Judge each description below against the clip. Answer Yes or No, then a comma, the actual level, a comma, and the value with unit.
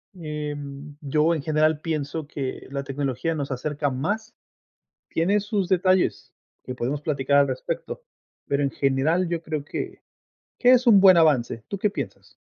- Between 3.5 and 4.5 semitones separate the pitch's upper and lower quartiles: Yes, average, 3.8 semitones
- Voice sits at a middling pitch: Yes, medium, 150 Hz